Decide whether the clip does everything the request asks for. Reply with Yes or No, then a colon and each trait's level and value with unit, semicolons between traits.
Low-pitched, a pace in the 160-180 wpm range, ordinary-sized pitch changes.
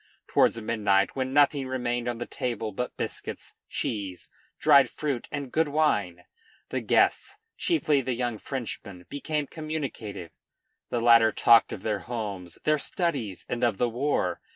No: low, 120 Hz; average, 150 wpm; average, 4.8 semitones